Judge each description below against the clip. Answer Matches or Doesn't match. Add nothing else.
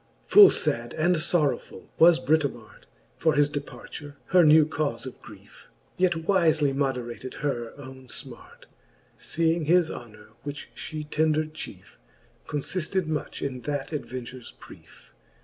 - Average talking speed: Doesn't match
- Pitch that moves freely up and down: Doesn't match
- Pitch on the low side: Doesn't match